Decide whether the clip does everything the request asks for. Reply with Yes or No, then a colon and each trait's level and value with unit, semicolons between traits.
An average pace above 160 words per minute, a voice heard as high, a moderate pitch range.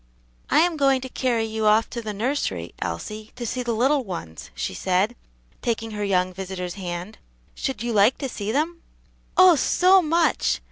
No: average, 180 wpm; high, 225 Hz; wide, 5.8 semitones